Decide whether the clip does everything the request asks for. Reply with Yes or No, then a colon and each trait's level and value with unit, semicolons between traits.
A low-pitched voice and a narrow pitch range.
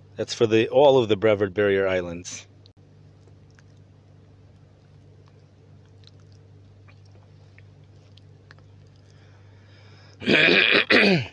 Yes: low, 105 Hz; narrow, 1.6 semitones